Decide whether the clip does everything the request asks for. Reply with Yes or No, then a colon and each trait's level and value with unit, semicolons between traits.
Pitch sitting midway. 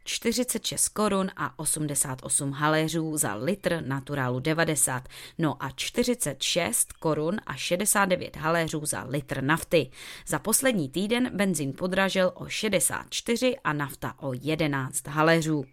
Yes: medium, 155 Hz